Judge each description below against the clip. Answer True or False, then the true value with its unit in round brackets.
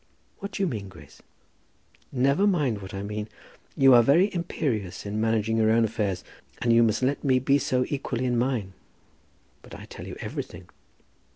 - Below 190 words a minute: True (180 wpm)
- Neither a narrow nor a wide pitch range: True (4.4 semitones)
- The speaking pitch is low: True (120 Hz)